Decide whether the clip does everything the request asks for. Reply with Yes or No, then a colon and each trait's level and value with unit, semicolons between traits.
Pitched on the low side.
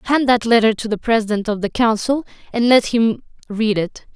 No: high, 225 Hz